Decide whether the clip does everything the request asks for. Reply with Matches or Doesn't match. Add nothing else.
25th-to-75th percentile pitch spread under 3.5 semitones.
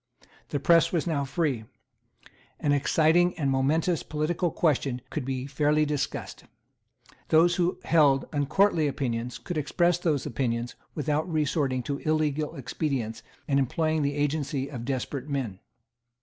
Matches